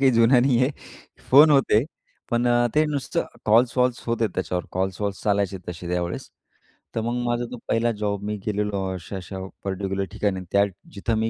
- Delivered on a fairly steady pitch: No, average, 3.7 semitones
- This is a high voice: No, low, 105 Hz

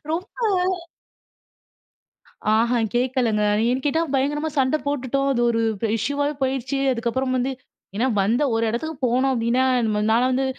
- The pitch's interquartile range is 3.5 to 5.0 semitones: No, average, 2.7 semitones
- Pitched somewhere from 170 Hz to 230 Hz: No, very high, 255 Hz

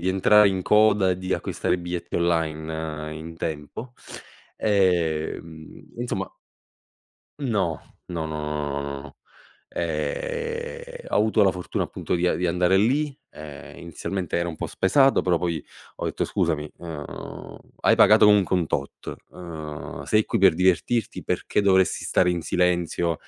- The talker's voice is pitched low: Yes, very low, 90 Hz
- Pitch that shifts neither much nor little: Yes, average, 3.8 semitones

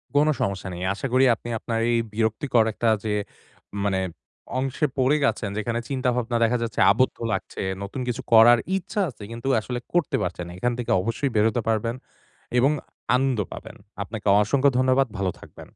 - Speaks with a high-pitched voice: No, low, 120 Hz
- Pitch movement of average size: Yes, average, 3.0 semitones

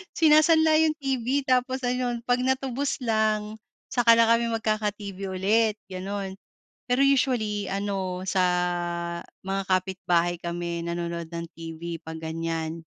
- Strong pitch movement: Yes, wide, 6.0 semitones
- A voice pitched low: No, high, 210 Hz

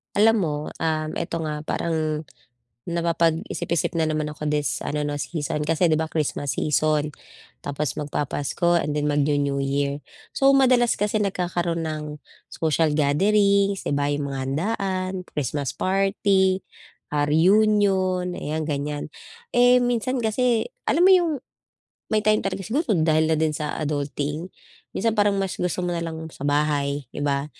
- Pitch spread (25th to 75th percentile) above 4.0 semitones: Yes, average, 4.7 semitones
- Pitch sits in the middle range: Yes, medium, 160 Hz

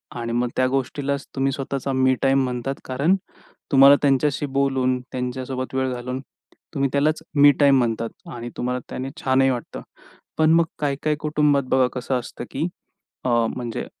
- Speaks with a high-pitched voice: No, low, 135 Hz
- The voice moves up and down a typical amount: No, narrow, 1.7 semitones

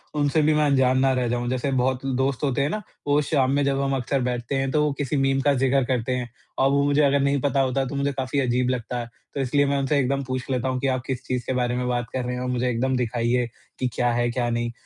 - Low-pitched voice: Yes, low, 130 Hz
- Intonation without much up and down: Yes, narrow, 1.9 semitones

